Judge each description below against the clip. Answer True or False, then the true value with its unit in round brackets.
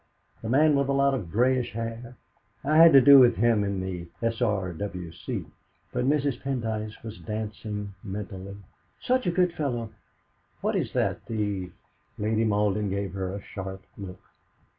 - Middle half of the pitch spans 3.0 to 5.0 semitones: True (4.6 semitones)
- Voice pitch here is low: True (110 Hz)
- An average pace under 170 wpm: True (160 wpm)